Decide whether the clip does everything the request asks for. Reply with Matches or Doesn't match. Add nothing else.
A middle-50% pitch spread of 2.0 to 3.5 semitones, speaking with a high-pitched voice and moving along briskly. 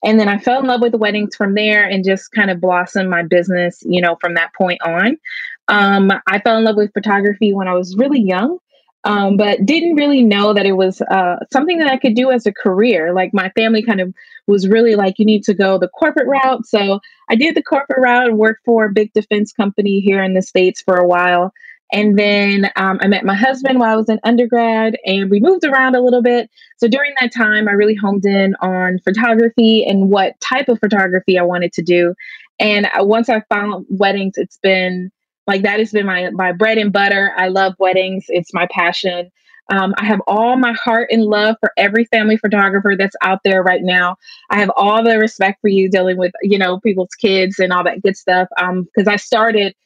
Matches